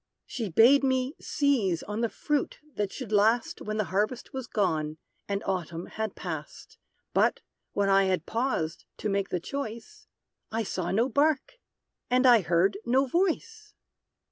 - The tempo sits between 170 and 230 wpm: No, average, 155 wpm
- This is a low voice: No, high, 220 Hz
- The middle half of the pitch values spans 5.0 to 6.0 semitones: Yes, wide, 5.4 semitones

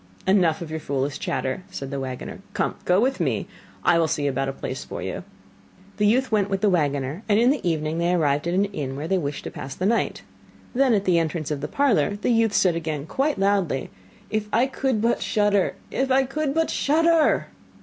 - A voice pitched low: No, medium, 185 Hz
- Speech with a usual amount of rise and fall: No, wide, 7.3 semitones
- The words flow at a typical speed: No, fast, 220 wpm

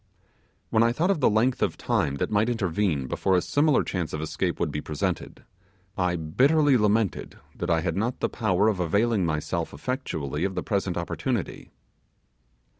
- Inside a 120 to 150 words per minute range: No, average, 175 wpm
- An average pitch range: No, wide, 6.1 semitones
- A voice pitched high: No, very low, 95 Hz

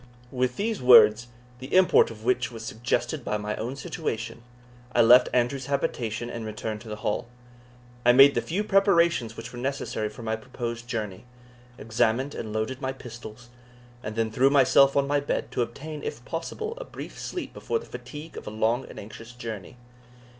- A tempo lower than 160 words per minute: No, average, 180 wpm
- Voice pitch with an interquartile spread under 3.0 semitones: No, average, 3.6 semitones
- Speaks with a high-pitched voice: No, low, 120 Hz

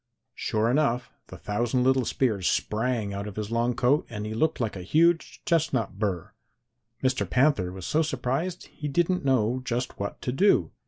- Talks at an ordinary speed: Yes, average, 175 wpm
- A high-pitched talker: No, low, 125 Hz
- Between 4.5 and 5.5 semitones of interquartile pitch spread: Yes, average, 4.8 semitones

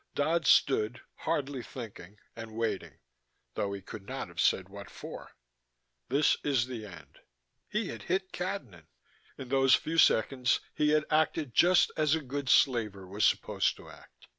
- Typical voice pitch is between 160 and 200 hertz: No, low, 125 Hz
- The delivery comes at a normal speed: Yes, average, 160 wpm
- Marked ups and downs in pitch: Yes, wide, 6.6 semitones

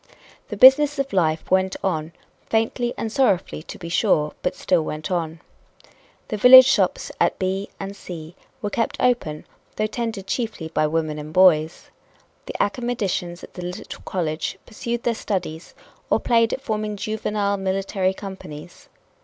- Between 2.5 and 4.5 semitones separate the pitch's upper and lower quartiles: No, average, 5.3 semitones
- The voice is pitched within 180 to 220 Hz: Yes, high, 190 Hz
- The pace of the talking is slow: No, average, 155 wpm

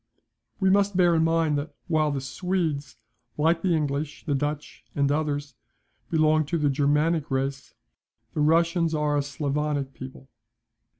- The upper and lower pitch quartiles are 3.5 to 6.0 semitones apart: No, narrow, 2.5 semitones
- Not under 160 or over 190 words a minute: No, average, 145 wpm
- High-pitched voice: No, medium, 150 Hz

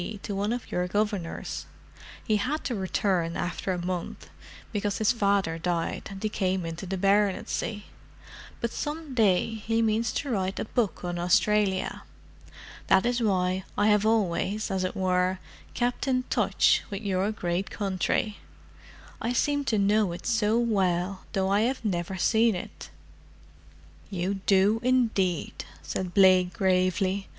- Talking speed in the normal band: Yes, average, 150 wpm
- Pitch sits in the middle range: No, high, 200 Hz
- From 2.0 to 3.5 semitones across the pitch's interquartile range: Yes, average, 3.0 semitones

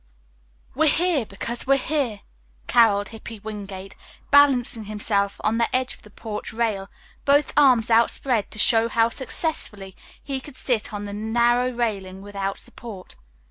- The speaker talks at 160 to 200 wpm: No, average, 145 wpm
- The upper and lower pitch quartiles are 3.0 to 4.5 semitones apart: Yes, average, 3.7 semitones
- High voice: Yes, high, 225 Hz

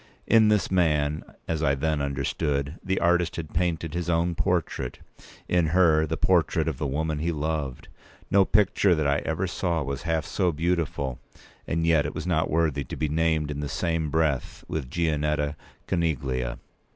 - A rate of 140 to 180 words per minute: Yes, average, 175 wpm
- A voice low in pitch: Yes, very low, 80 Hz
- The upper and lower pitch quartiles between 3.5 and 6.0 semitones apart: No, average, 2.7 semitones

